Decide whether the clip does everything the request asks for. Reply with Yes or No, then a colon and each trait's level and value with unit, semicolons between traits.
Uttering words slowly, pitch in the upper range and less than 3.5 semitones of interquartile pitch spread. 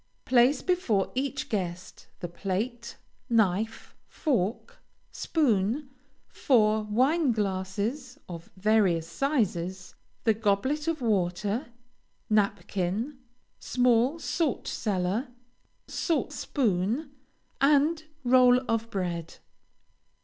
No: slow, 85 wpm; high, 225 Hz; wide, 5.5 semitones